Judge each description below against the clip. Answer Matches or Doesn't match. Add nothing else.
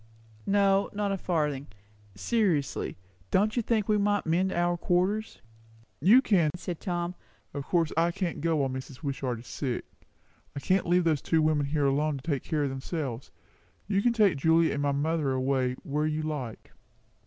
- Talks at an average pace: Matches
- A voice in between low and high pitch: Matches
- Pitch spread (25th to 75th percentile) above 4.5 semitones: Matches